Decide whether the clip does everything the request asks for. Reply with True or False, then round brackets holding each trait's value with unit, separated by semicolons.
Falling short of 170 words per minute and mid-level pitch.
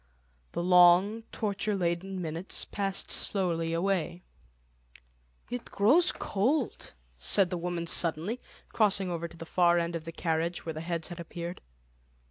True (140 wpm; 175 Hz)